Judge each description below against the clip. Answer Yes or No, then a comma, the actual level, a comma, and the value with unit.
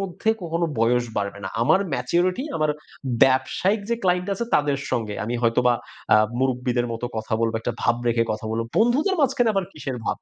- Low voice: Yes, low, 130 Hz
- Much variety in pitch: Yes, wide, 7.7 semitones